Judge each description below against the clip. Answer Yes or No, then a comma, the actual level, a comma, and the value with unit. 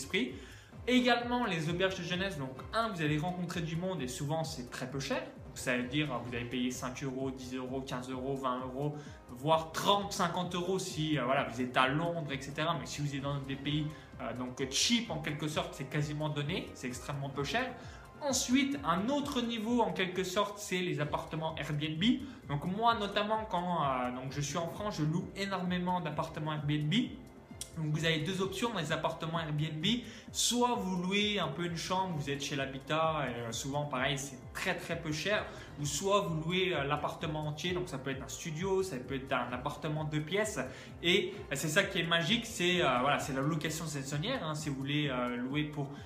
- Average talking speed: Yes, average, 200 wpm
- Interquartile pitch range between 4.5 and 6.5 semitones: Yes, average, 5.1 semitones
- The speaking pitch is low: No, medium, 155 Hz